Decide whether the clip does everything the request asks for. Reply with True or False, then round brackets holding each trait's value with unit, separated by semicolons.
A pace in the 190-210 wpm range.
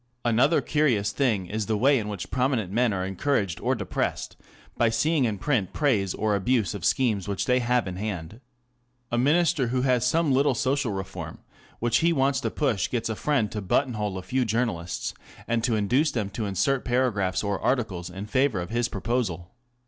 True (195 wpm)